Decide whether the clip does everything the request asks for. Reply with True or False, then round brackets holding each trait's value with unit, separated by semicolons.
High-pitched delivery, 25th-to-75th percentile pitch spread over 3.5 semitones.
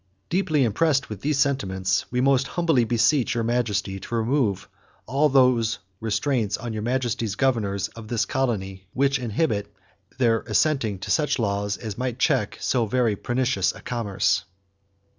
False (120 Hz; 4.1 semitones)